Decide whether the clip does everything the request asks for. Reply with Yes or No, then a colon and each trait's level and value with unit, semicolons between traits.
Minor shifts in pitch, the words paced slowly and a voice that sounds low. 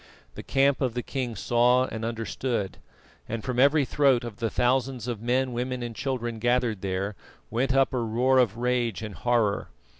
No: narrow, 2.2 semitones; average, 180 wpm; low, 120 Hz